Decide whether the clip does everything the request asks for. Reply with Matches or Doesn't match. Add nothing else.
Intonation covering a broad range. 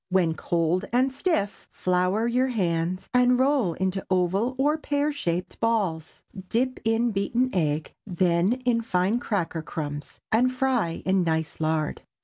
Matches